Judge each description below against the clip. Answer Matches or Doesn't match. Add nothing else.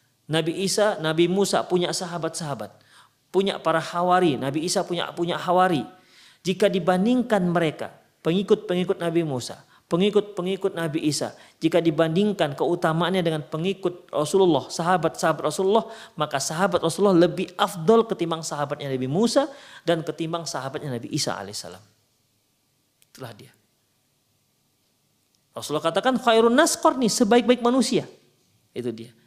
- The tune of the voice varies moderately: Matches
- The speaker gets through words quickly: Doesn't match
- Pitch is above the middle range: Doesn't match